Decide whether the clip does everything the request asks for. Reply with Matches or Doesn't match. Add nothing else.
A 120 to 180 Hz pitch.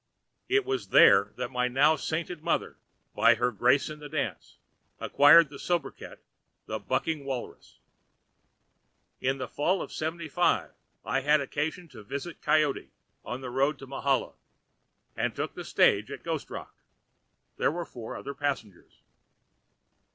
Matches